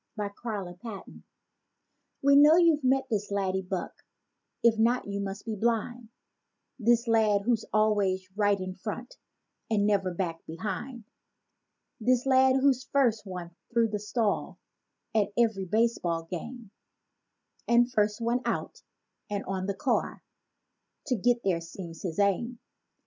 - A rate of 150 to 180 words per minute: No, slow, 135 wpm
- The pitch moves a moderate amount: Yes, average, 3.7 semitones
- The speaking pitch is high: Yes, high, 215 Hz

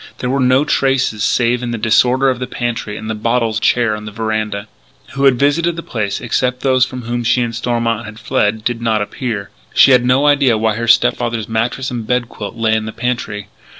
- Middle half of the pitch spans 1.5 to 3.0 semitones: Yes, narrow, 2.4 semitones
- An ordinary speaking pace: No, fast, 225 wpm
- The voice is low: Yes, low, 120 Hz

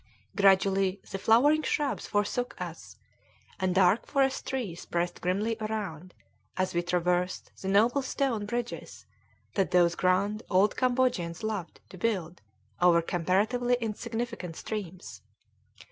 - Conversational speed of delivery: No, slow, 120 wpm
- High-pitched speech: Yes, high, 200 Hz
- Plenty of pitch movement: No, average, 4.4 semitones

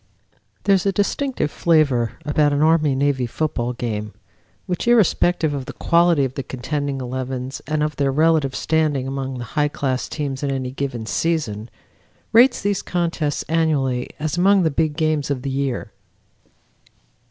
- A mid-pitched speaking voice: Yes, medium, 145 Hz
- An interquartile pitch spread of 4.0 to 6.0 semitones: No, average, 3.6 semitones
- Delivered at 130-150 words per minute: No, average, 160 wpm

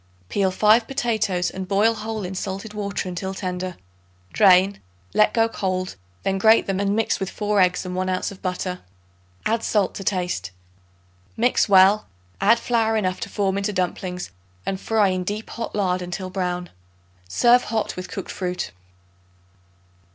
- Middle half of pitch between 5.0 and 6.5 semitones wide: No, narrow, 2.6 semitones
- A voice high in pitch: Yes, high, 195 Hz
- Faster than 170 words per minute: No, average, 160 wpm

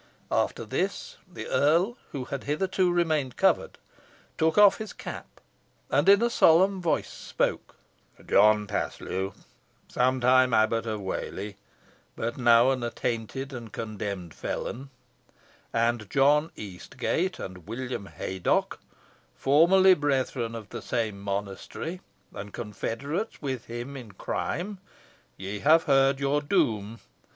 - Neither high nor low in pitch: No, low, 130 Hz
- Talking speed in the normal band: No, slow, 120 wpm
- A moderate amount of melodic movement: No, wide, 6.1 semitones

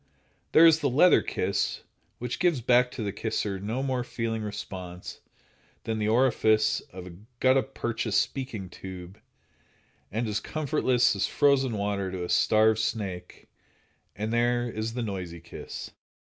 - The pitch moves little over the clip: No, average, 3.9 semitones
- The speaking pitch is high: No, low, 110 Hz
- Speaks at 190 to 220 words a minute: No, average, 150 wpm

